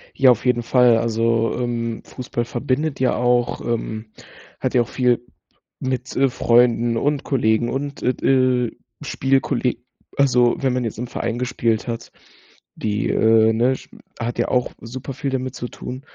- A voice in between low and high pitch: No, low, 125 Hz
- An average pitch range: No, narrow, 1.8 semitones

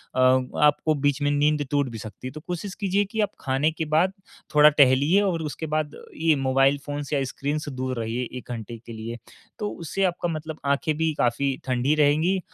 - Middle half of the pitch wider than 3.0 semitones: Yes, average, 3.6 semitones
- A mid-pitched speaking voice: Yes, medium, 145 Hz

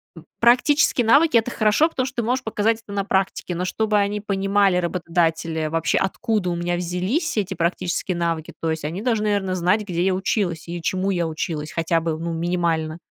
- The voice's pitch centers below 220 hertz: Yes, medium, 185 Hz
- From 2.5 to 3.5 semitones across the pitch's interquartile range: No, average, 3.9 semitones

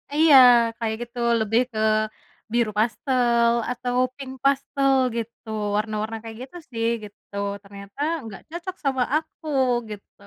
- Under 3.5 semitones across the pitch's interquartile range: No, average, 3.8 semitones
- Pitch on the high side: Yes, high, 235 Hz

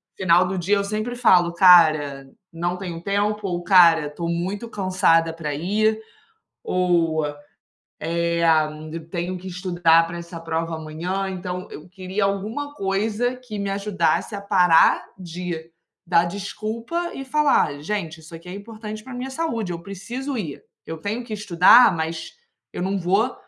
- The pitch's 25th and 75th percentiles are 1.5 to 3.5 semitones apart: No, average, 3.9 semitones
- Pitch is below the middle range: No, medium, 185 Hz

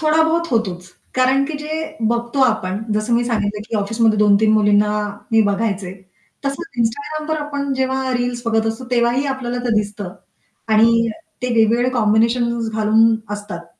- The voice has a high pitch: Yes, high, 230 Hz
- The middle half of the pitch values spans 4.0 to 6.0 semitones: No, average, 3.4 semitones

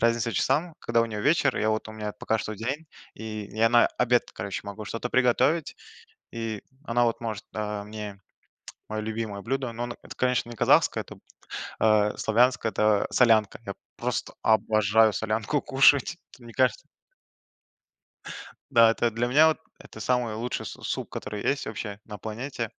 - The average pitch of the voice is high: No, low, 115 Hz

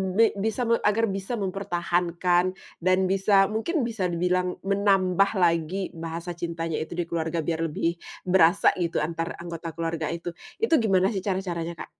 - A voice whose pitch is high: No, medium, 180 Hz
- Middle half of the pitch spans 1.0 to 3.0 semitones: Yes, average, 2.7 semitones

